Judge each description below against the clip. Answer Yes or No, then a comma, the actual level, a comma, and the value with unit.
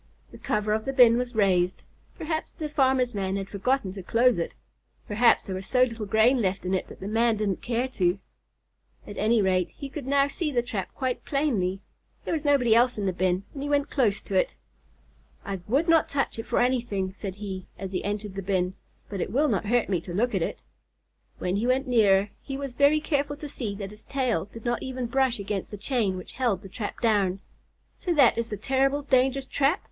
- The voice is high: Yes, high, 230 Hz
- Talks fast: Yes, fast, 225 wpm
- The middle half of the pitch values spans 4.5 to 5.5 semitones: Yes, average, 5.2 semitones